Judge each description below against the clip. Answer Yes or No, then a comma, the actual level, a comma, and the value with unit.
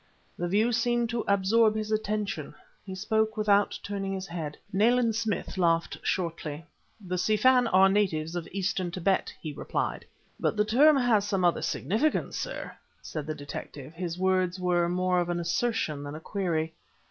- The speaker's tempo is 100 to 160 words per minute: No, average, 170 wpm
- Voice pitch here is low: No, high, 190 Hz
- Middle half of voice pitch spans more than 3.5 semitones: Yes, average, 4.0 semitones